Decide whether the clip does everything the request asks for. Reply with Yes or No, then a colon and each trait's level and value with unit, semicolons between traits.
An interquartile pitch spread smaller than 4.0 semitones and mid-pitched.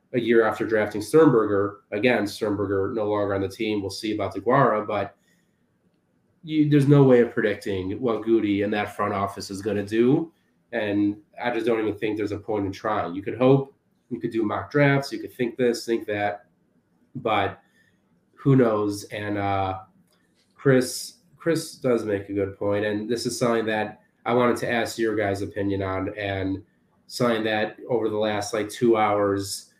No: average, 2.7 semitones; low, 105 Hz